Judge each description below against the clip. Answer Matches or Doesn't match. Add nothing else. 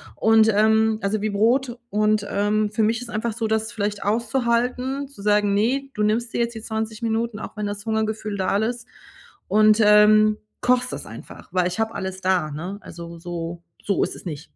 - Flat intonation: Matches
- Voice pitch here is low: Doesn't match